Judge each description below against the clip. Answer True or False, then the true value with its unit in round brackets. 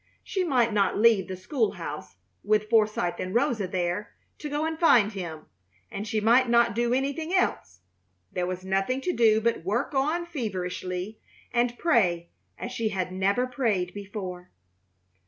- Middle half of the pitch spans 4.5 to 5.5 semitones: True (5.0 semitones)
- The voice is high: True (215 Hz)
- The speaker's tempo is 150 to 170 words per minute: True (160 wpm)